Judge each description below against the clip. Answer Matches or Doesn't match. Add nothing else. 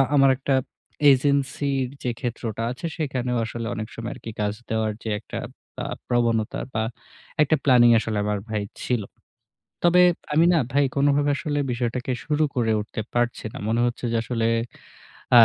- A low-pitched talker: Matches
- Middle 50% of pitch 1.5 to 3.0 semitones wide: Doesn't match